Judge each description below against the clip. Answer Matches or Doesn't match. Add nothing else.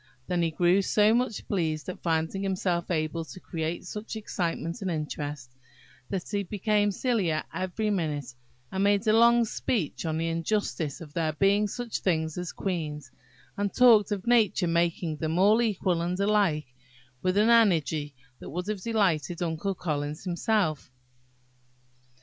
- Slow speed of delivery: Doesn't match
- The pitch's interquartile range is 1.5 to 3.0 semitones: Doesn't match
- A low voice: Doesn't match